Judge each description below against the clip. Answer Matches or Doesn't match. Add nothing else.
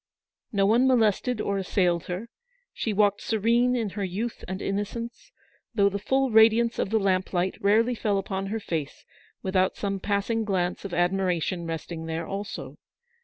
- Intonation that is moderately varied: Matches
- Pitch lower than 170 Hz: Doesn't match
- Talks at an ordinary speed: Matches